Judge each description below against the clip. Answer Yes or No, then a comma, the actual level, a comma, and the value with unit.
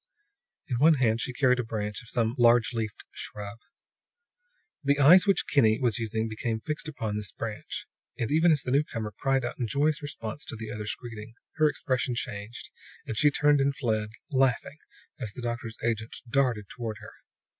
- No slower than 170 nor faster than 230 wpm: Yes, average, 180 wpm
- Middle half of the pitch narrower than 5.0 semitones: Yes, average, 3.8 semitones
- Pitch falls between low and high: No, low, 120 Hz